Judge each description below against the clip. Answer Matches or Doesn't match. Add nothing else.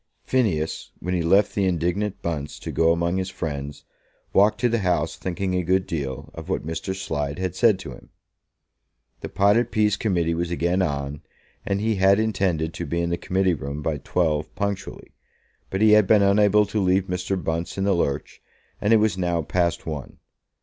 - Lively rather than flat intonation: Doesn't match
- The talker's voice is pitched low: Matches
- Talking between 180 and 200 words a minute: Matches